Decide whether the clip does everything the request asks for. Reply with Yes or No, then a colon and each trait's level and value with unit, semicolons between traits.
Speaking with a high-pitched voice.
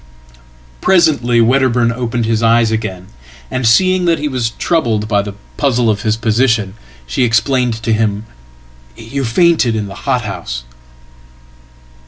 No: low, 115 Hz